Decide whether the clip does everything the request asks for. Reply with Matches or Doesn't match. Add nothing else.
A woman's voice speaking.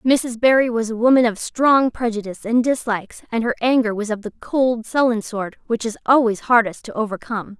Matches